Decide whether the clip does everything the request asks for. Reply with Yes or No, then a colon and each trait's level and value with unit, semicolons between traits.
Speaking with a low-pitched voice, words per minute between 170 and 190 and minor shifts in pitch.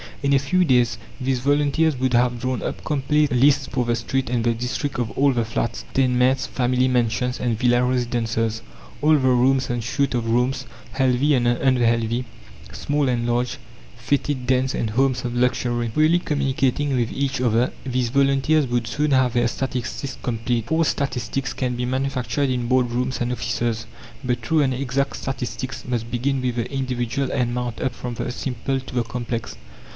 Yes: low, 125 Hz; average, 180 wpm; narrow, 2.0 semitones